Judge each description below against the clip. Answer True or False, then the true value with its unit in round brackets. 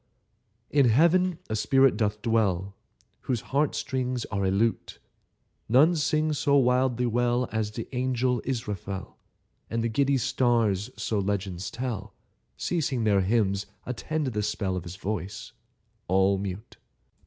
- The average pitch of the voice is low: True (115 Hz)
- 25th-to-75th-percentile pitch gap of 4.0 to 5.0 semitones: True (4.4 semitones)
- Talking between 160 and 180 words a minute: False (140 wpm)